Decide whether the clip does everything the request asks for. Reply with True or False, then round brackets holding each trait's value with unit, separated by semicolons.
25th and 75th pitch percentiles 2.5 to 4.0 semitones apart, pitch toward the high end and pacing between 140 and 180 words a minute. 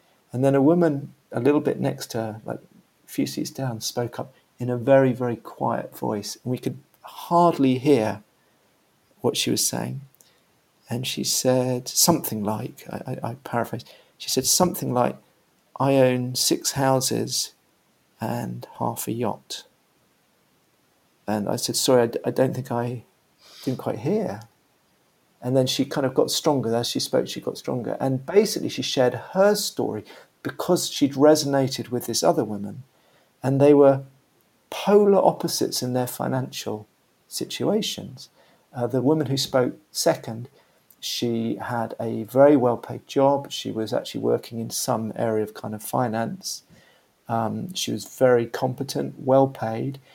False (3.0 semitones; 130 Hz; 160 wpm)